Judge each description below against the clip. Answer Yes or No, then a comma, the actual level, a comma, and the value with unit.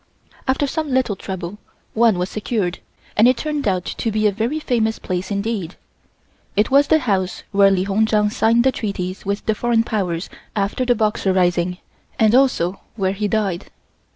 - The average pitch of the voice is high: Yes, high, 210 Hz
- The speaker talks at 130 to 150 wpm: No, average, 180 wpm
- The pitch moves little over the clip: No, average, 3.6 semitones